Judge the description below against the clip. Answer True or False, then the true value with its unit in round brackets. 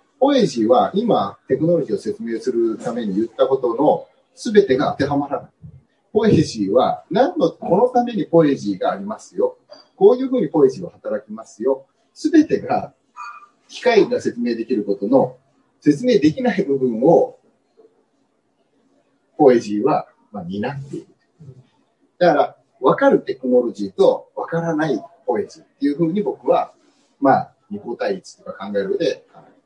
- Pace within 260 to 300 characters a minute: False (310 characters per minute)